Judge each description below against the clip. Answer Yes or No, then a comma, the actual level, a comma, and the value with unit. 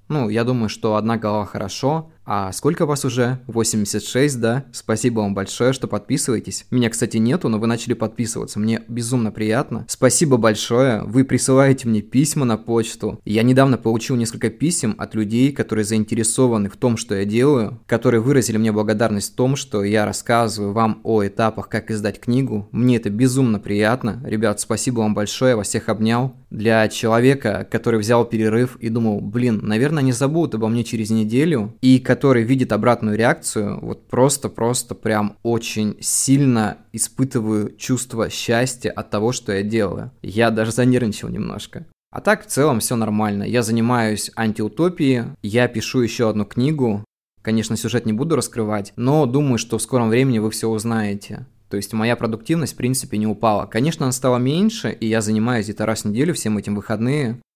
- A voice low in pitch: Yes, low, 115 Hz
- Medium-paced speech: No, fast, 170 wpm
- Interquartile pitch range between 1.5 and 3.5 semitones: Yes, average, 2.7 semitones